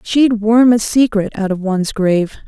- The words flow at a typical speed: Yes, average, 195 wpm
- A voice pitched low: No, high, 215 Hz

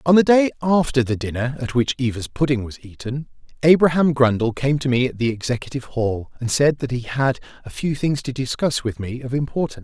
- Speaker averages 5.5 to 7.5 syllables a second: Yes, 5.8 syllables/s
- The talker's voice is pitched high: No, low, 130 Hz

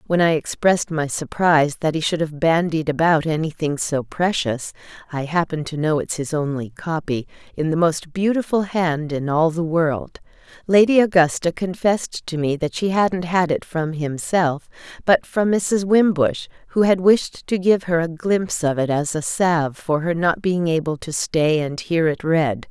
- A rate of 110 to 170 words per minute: No, average, 185 wpm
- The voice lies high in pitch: No, medium, 165 Hz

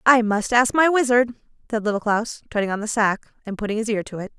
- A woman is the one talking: Yes, female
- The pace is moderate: No, fast, 245 wpm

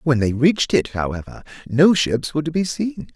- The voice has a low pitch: No, medium, 145 Hz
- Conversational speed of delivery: No, fast, 210 wpm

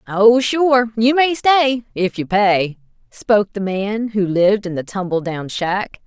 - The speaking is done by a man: No, female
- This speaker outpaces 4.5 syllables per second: No, 4.2 syllables/s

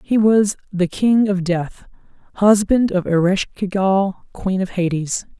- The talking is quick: No, average, 155 wpm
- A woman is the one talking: Yes, female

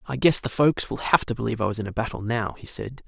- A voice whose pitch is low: Yes, low, 120 Hz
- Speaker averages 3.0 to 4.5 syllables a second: No, 6.7 syllables/s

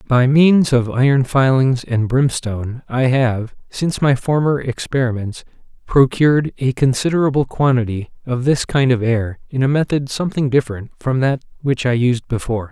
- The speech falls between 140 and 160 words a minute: Yes, average, 155 wpm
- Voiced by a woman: No, male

